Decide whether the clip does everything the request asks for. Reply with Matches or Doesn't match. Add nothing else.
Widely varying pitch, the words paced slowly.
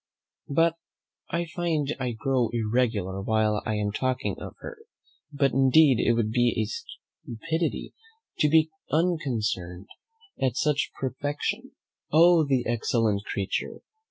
Matches